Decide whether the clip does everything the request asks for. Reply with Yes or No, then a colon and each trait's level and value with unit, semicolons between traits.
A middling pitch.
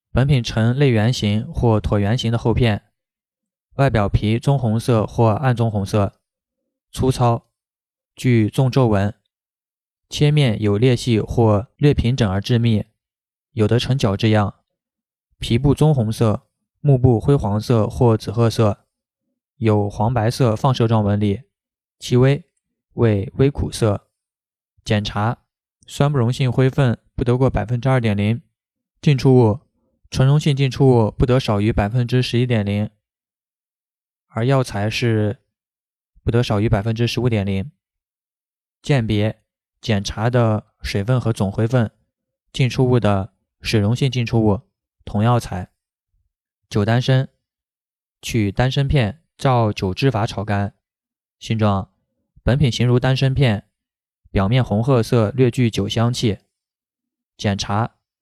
No: low, 115 Hz